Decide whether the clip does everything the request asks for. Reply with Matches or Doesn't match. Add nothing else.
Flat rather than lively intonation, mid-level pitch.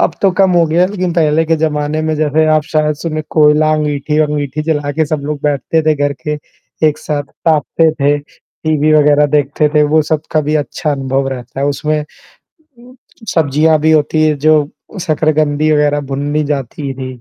Matches